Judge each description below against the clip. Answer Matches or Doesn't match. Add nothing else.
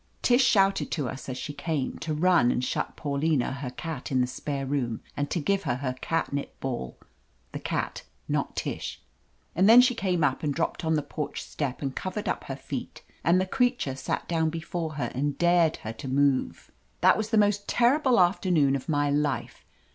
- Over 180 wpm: Matches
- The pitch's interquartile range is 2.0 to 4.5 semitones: Doesn't match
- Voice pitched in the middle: Matches